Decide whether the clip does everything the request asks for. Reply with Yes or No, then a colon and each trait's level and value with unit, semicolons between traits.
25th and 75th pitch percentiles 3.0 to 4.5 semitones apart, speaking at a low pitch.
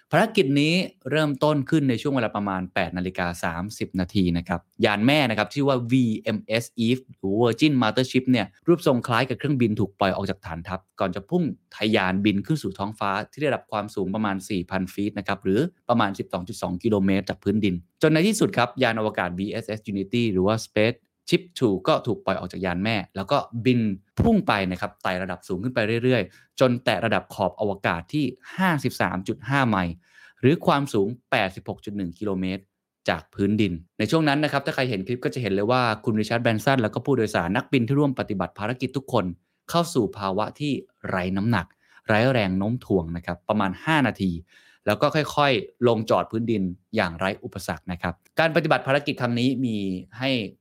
No: average, 5.3 semitones; low, 110 Hz